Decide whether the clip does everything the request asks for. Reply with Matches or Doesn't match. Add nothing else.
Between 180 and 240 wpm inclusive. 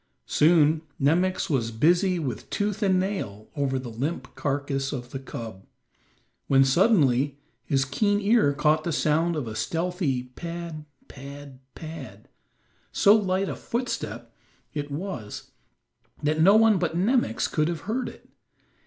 Doesn't match